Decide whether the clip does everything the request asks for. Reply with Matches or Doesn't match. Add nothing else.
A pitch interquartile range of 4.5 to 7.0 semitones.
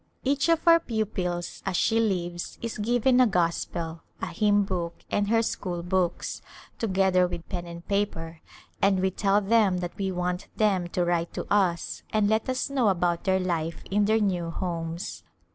Doesn't match